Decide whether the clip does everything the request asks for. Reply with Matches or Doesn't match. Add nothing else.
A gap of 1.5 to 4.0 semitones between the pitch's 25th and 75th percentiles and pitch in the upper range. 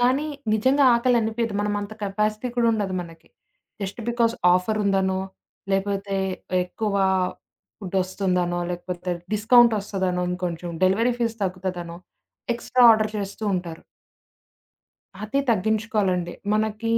Matches